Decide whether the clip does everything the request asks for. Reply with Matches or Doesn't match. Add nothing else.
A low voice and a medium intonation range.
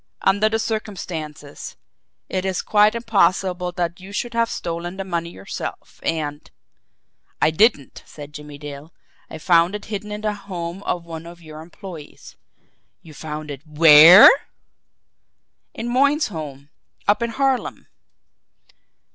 Doesn't match